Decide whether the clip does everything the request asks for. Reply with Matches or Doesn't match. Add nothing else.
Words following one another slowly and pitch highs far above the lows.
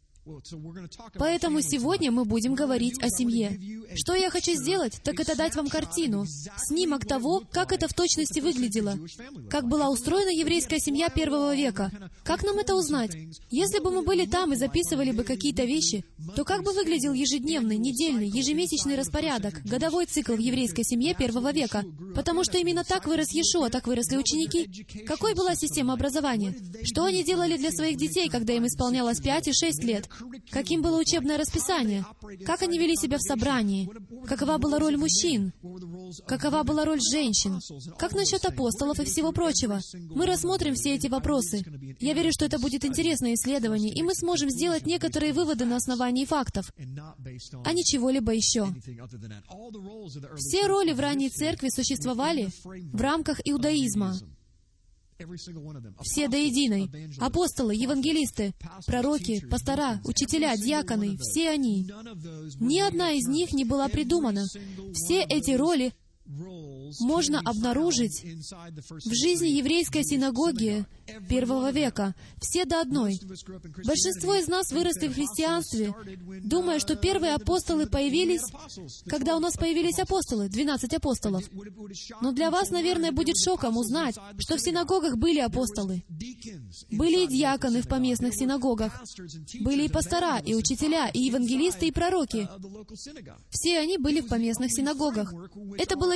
Doesn't match